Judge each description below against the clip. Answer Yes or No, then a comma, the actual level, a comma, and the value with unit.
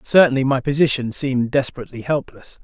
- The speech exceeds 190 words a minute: No, slow, 135 wpm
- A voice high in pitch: No, low, 135 Hz